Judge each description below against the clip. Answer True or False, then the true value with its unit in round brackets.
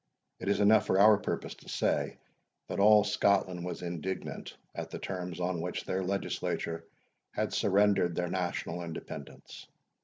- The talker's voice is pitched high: False (95 Hz)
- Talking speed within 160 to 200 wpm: False (150 wpm)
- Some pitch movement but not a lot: False (2.3 semitones)